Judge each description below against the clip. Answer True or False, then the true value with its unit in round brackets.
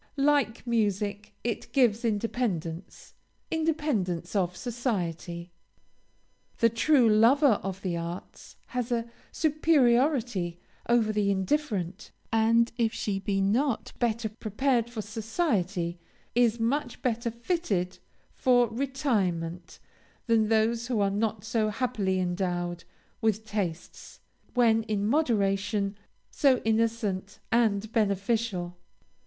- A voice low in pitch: False (220 Hz)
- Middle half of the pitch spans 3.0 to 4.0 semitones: True (3.6 semitones)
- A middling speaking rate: False (105 wpm)